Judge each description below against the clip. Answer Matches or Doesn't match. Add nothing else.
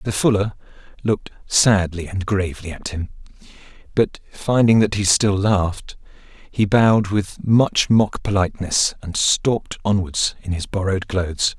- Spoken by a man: Matches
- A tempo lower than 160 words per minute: Matches